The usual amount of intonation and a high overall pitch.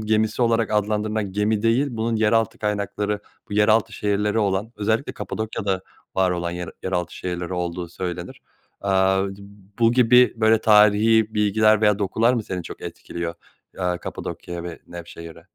No: average, 3.0 semitones; low, 105 Hz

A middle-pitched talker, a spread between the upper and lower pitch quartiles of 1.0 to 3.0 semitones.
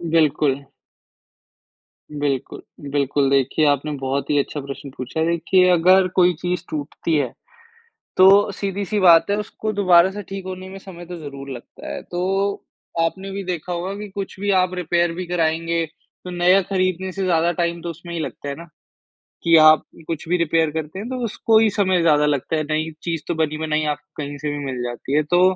No: medium, 170 Hz; average, 3.7 semitones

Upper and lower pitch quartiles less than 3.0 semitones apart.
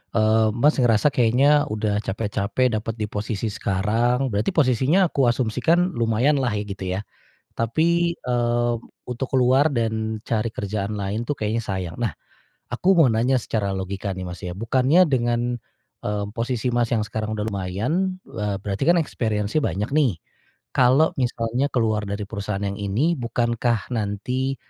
No: average, 3.5 semitones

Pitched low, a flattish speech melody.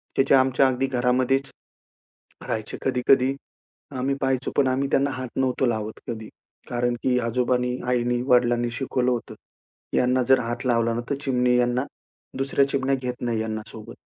Yes: low, 125 Hz; narrow, 1.6 semitones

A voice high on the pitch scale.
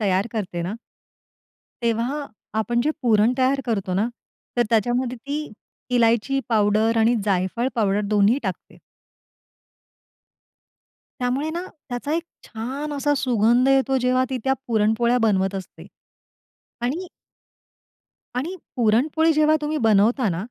Yes: high, 240 Hz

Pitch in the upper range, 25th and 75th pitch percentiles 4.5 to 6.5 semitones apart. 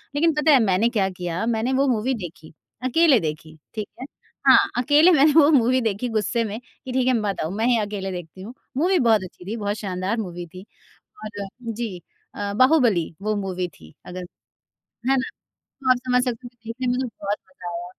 Yes: high, 220 Hz; wide, 5.4 semitones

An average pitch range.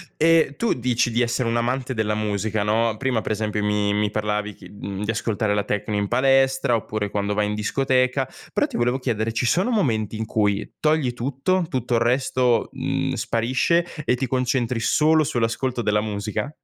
Yes: average, 3.6 semitones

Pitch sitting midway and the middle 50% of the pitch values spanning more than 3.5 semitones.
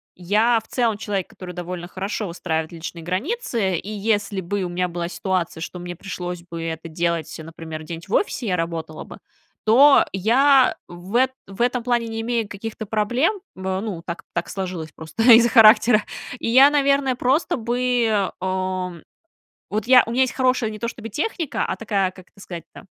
No: high, 200 Hz; average, 5.1 semitones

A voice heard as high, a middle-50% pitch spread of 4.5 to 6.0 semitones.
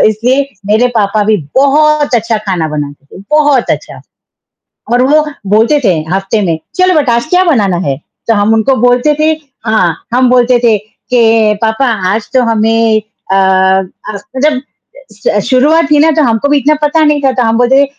Yes: high, 235 Hz; average, 5.0 semitones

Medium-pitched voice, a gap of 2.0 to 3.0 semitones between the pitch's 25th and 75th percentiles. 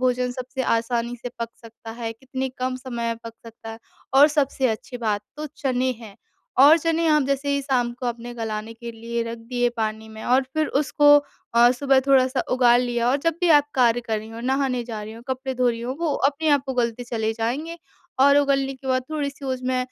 No: very high, 250 Hz; average, 2.7 semitones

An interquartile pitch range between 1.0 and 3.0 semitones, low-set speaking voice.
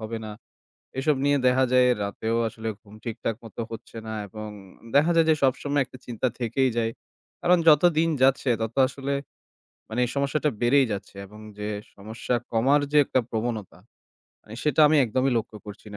No: average, 4.0 semitones; low, 120 Hz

